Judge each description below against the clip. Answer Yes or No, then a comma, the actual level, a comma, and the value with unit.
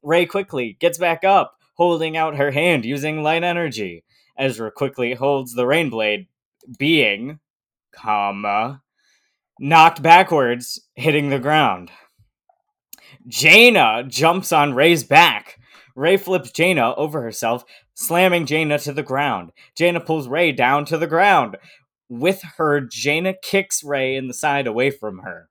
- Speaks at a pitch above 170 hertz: No, medium, 150 Hz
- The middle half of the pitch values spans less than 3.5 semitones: No, average, 5.0 semitones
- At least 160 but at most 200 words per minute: No, slow, 135 wpm